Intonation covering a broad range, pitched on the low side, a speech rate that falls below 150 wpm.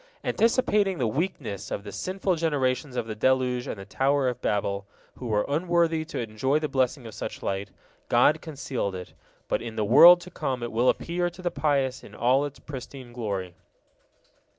No: wide, 6.1 semitones; low, 130 Hz; average, 185 wpm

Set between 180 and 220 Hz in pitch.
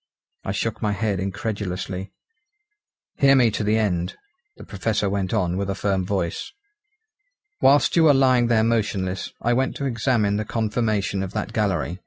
No: low, 105 Hz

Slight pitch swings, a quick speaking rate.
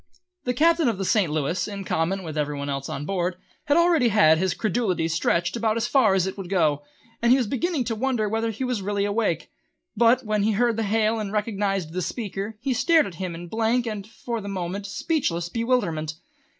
No: average, 4.7 semitones; fast, 215 wpm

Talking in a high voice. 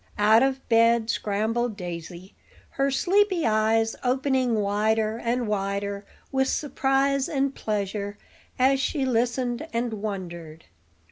Yes: high, 230 Hz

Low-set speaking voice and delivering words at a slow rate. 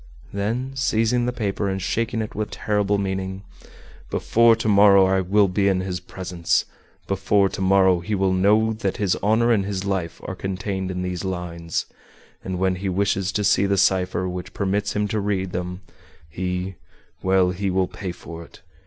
No: very low, 95 Hz; average, 180 wpm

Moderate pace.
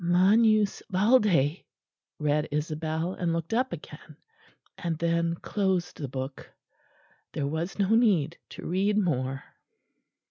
No: slow, 120 wpm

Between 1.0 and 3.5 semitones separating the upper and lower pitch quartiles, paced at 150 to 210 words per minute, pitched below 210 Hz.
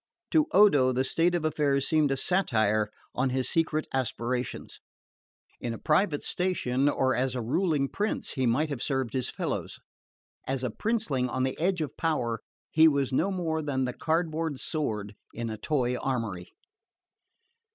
No: average, 4.1 semitones; average, 160 wpm; low, 135 Hz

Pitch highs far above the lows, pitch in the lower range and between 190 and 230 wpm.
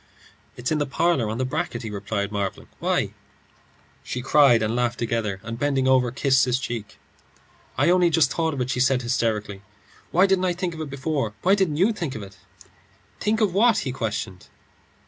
Yes: wide, 6.1 semitones; low, 130 Hz; average, 195 wpm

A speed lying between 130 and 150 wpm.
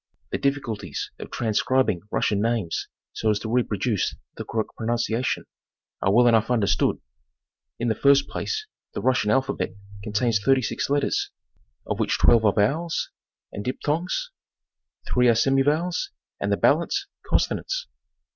Yes: average, 140 wpm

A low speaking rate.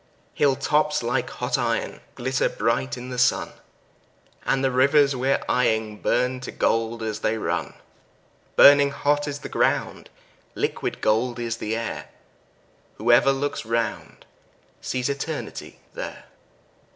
Yes: slow, 130 wpm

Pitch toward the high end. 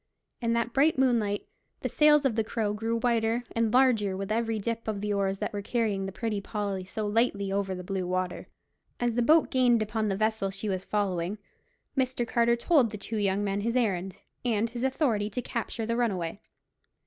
Yes: high, 220 Hz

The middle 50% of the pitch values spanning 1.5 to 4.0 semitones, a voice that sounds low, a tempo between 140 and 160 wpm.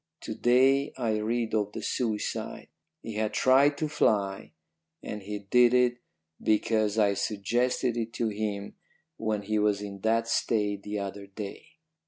Yes: average, 2.8 semitones; low, 110 Hz; average, 155 wpm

